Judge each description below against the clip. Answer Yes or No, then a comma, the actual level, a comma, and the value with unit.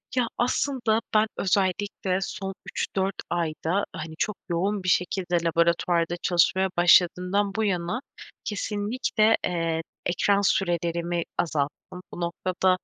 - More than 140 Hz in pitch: Yes, medium, 185 Hz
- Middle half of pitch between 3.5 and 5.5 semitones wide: No, average, 3.0 semitones